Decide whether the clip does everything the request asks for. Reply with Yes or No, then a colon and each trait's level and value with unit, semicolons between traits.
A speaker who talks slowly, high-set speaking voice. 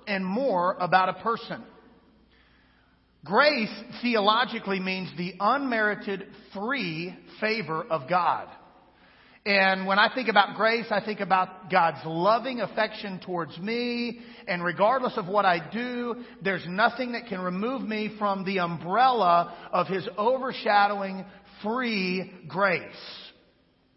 Yes: slow, 120 wpm; high, 205 Hz